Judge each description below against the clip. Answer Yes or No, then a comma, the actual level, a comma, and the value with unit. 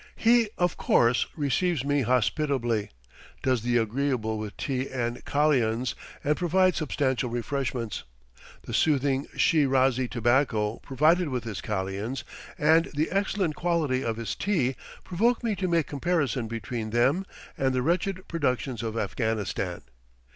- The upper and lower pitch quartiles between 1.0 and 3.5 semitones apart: No, average, 5.2 semitones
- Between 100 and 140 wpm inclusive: Yes, slow, 135 wpm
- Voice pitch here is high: No, low, 130 Hz